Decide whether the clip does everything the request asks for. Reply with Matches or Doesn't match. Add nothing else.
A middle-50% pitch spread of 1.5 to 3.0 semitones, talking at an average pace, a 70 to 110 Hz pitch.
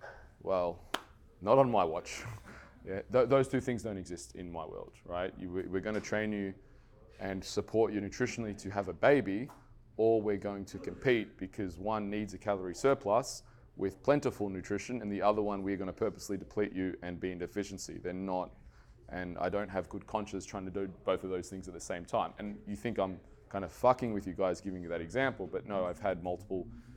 Doesn't match